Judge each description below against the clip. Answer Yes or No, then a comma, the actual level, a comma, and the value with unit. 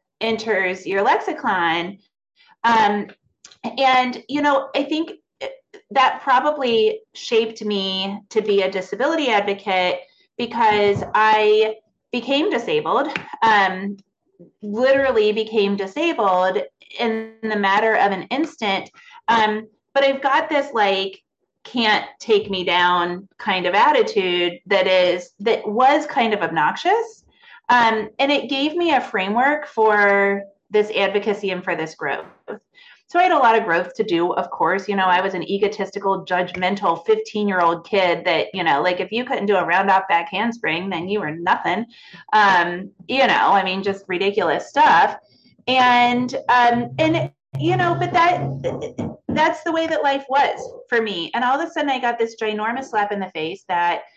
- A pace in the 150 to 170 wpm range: Yes, average, 155 wpm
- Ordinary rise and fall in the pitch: No, wide, 5.9 semitones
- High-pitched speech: Yes, high, 215 Hz